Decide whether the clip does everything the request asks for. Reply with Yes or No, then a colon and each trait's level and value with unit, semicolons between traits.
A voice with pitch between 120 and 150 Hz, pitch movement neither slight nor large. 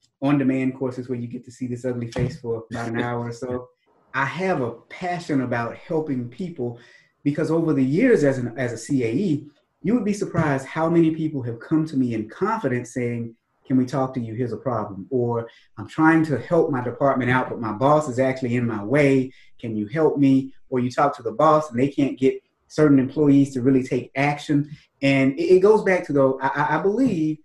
Yes: low, 135 Hz; average, 3.5 semitones